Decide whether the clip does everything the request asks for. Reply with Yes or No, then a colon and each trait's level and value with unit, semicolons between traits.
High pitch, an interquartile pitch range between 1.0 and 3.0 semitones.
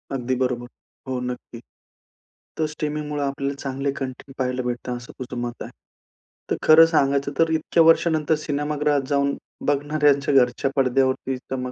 No: medium, 140 Hz; narrow, 2.6 semitones